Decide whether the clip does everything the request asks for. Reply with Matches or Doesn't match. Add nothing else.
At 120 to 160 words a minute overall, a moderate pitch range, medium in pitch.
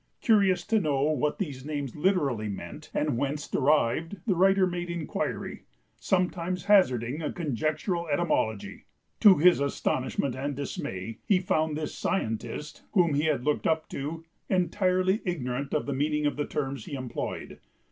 Matches